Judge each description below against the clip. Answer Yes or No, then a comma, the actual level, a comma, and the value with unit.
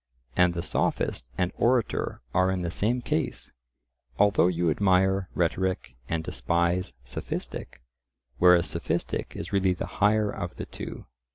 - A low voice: Yes, very low, 90 Hz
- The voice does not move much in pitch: Yes, narrow, 2.2 semitones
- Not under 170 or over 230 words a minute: No, slow, 135 wpm